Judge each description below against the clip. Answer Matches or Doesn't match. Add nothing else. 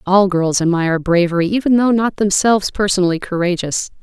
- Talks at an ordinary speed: Matches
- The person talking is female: Matches